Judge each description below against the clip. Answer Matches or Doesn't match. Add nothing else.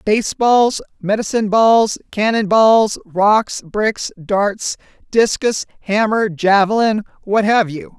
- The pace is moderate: Doesn't match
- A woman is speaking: Matches